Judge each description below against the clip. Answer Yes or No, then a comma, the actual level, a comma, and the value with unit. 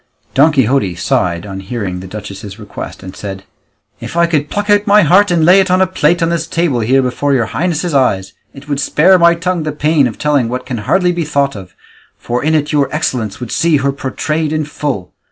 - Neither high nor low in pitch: Yes, medium, 145 Hz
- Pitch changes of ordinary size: No, wide, 6.5 semitones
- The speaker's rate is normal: No, fast, 225 wpm